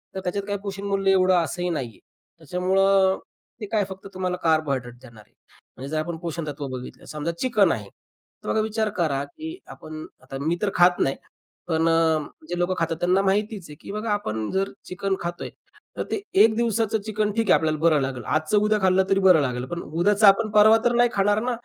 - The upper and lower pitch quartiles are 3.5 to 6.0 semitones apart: Yes, average, 4.6 semitones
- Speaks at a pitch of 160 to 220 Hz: Yes, medium, 185 Hz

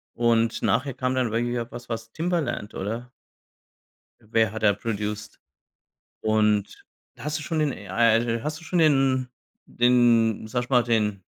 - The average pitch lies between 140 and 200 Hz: No, low, 115 Hz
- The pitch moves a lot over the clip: No, average, 2.8 semitones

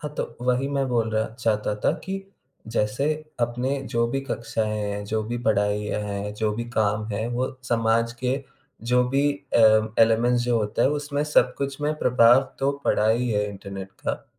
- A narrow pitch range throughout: No, average, 3.5 semitones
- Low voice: Yes, low, 115 Hz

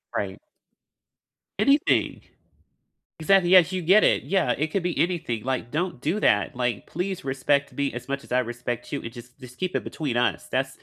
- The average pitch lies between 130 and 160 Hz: Yes, medium, 140 Hz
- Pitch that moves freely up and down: Yes, wide, 6.5 semitones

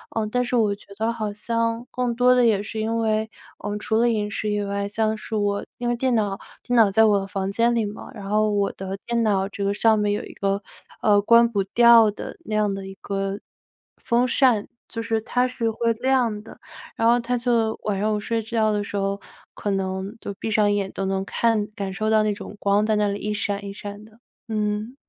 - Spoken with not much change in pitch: Yes, narrow, 2.2 semitones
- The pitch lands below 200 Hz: No, high, 215 Hz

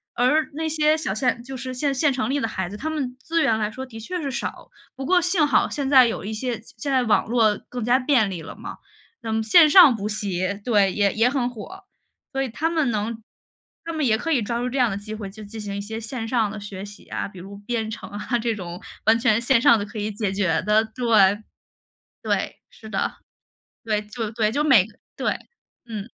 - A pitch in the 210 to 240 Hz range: Yes, high, 225 Hz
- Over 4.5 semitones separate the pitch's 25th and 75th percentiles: No, average, 4.1 semitones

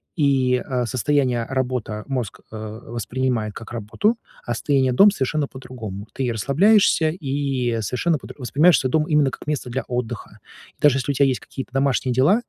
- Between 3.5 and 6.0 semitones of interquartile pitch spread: No, average, 3.0 semitones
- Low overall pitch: Yes, low, 130 Hz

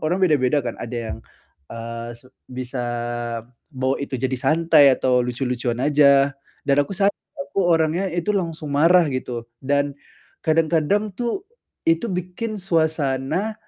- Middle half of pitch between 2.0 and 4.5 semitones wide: No, average, 4.9 semitones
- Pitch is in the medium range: Yes, medium, 150 Hz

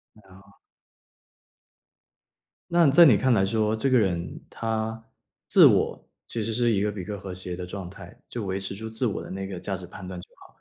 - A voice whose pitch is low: Yes, low, 100 Hz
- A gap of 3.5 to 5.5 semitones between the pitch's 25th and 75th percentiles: No, average, 3.1 semitones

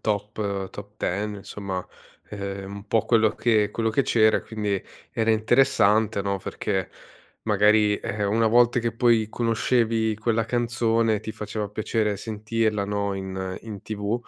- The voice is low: Yes, low, 110 Hz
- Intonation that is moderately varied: No, narrow, 1.9 semitones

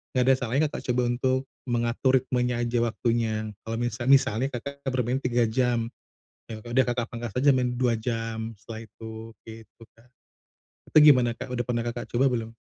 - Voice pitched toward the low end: Yes, low, 120 Hz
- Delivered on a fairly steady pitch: Yes, narrow, 1.9 semitones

